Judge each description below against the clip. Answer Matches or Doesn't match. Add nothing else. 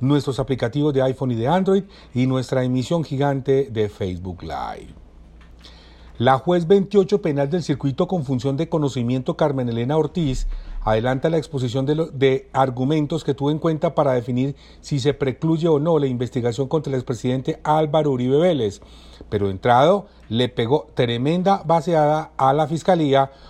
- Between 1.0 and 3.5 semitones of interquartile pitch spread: Doesn't match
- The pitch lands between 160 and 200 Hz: Doesn't match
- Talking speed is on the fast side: Doesn't match